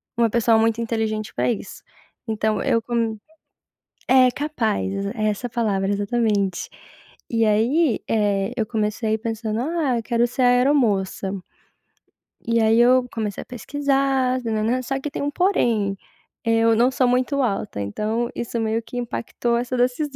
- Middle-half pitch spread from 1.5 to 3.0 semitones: Yes, narrow, 2.6 semitones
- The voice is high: Yes, high, 230 Hz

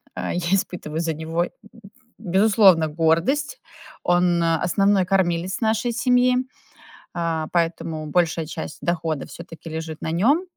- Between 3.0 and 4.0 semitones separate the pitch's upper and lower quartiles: Yes, average, 3.4 semitones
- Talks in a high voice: No, medium, 170 Hz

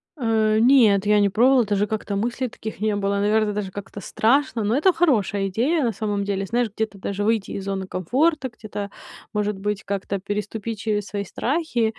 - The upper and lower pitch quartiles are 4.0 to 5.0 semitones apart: No, average, 2.7 semitones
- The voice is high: Yes, high, 210 Hz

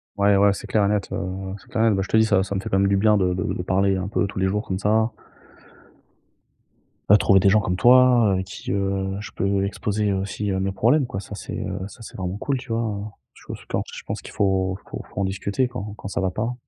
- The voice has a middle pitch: No, low, 100 Hz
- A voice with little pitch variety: Yes, narrow, 1.9 semitones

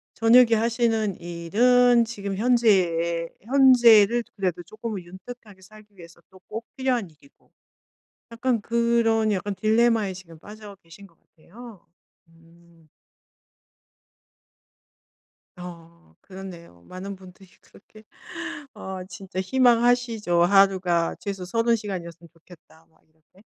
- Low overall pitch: No, high, 195 Hz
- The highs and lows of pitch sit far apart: No, average, 4.9 semitones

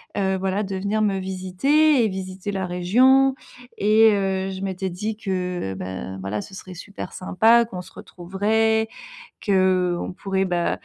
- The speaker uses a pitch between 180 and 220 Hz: Yes, high, 190 Hz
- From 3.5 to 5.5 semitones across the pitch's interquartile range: No, average, 2.7 semitones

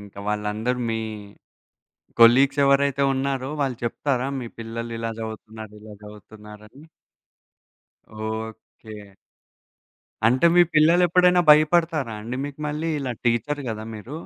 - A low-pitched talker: Yes, low, 120 Hz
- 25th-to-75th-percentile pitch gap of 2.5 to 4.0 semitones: No, average, 4.4 semitones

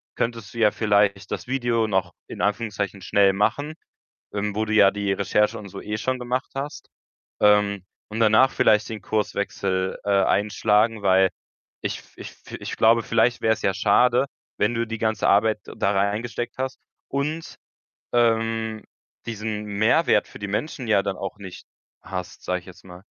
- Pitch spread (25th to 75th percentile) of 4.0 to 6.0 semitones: No, narrow, 2.4 semitones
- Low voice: Yes, low, 105 Hz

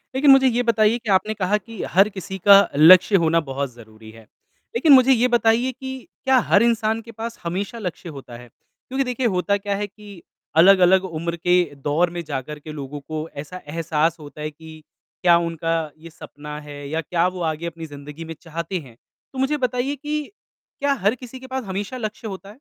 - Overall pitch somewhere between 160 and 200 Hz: Yes, medium, 185 Hz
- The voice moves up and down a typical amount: No, wide, 6.4 semitones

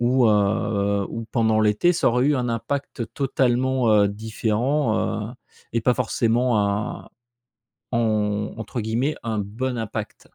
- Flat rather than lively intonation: No, average, 3.1 semitones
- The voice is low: Yes, low, 115 Hz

